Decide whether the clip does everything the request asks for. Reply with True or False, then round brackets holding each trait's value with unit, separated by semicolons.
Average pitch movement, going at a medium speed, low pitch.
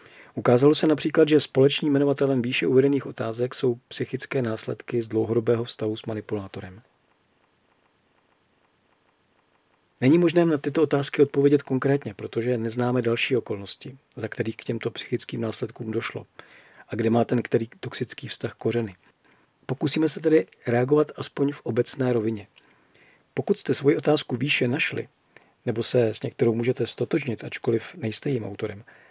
True (3.6 semitones; 140 wpm; 125 Hz)